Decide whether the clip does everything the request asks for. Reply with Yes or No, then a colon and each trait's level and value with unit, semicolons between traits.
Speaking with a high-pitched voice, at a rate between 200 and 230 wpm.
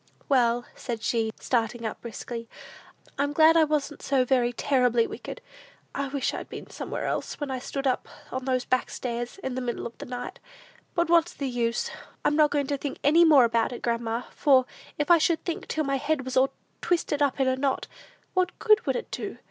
Yes: very high, 265 Hz; fast, 205 wpm